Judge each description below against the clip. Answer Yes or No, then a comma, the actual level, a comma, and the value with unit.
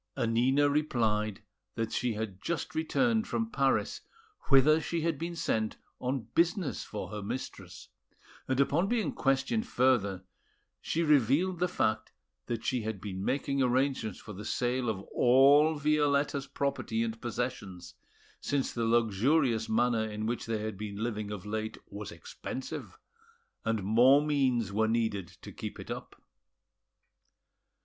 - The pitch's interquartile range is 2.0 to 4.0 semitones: No, average, 4.7 semitones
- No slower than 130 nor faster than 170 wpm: Yes, average, 140 wpm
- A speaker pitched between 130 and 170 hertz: No, low, 120 Hz